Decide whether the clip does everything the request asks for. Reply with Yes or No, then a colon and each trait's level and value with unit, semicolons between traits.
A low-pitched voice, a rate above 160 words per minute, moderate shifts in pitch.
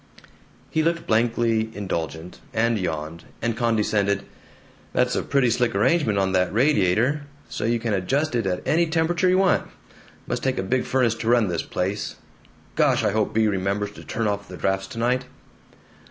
Yes: low, 110 Hz; average, 170 wpm; average, 4.4 semitones